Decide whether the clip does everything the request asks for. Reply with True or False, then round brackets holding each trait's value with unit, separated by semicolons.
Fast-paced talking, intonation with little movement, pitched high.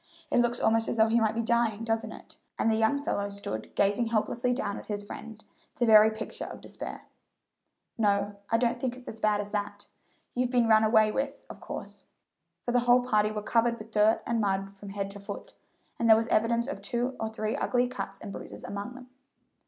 True (215 wpm; 2.3 semitones; 220 Hz)